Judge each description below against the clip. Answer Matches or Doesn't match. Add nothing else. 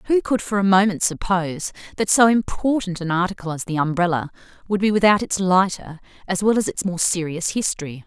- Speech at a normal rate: Matches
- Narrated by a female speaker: Matches